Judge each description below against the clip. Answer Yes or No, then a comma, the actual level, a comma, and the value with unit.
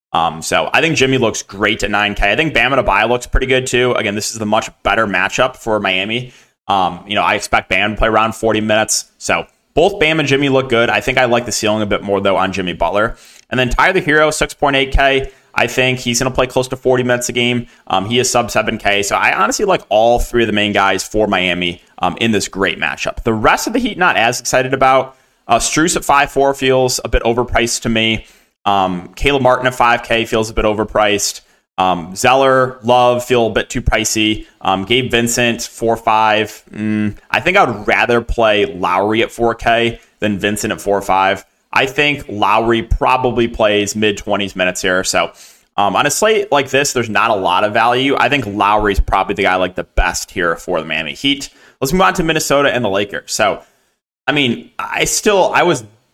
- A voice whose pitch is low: Yes, low, 115 Hz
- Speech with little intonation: No, average, 3.8 semitones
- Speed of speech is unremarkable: No, fast, 215 wpm